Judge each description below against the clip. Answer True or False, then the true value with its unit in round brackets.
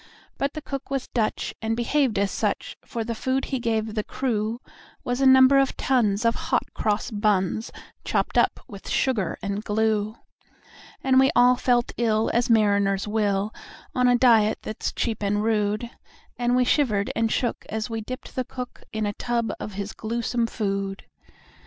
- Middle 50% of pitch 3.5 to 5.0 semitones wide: False (2.9 semitones)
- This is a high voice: True (225 Hz)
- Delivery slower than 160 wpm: False (175 wpm)